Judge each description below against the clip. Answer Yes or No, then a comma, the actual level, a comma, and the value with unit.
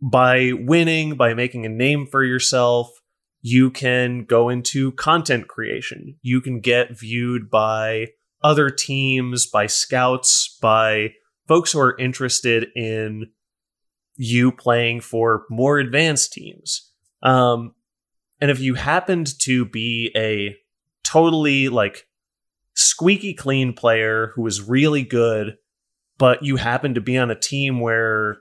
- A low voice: Yes, low, 125 Hz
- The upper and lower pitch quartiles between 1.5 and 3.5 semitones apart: Yes, average, 3.1 semitones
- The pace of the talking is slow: Yes, slow, 130 wpm